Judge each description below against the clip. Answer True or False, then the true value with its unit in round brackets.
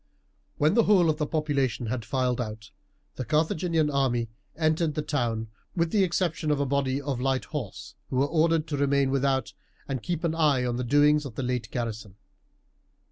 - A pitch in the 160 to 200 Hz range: False (140 Hz)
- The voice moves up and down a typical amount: True (3.7 semitones)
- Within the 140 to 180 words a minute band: False (190 wpm)